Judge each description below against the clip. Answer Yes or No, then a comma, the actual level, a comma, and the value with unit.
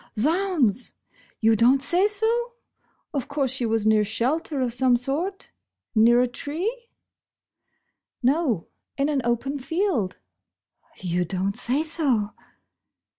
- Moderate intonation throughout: No, wide, 6.3 semitones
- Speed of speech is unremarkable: No, slow, 130 wpm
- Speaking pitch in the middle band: No, very high, 265 Hz